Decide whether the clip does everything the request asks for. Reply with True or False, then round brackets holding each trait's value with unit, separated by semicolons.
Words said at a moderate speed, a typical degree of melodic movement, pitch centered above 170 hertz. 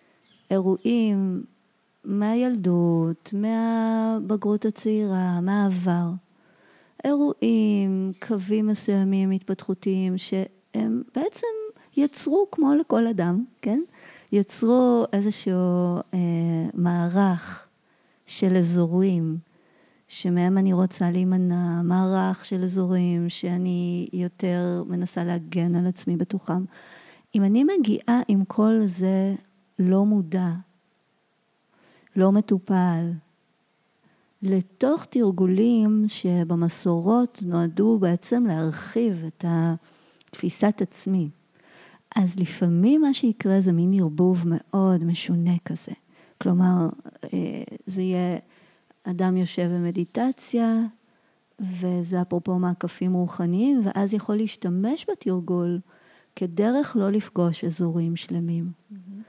False (85 wpm; 3.4 semitones; 190 Hz)